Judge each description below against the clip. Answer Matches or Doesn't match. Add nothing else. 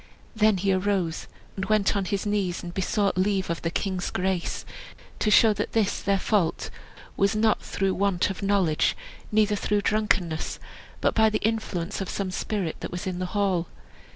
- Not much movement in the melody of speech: Matches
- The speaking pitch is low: Doesn't match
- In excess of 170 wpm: Matches